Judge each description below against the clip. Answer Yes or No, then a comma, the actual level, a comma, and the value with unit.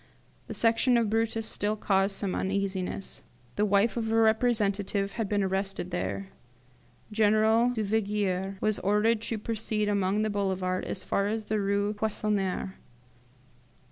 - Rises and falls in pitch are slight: Yes, narrow, 2.0 semitones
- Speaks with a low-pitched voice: No, high, 205 Hz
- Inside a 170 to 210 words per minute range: No, average, 140 wpm